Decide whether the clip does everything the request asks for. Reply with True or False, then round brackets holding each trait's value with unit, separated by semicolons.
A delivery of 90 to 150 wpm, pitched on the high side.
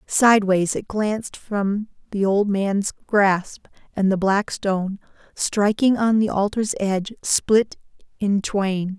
True (135 wpm; 200 Hz)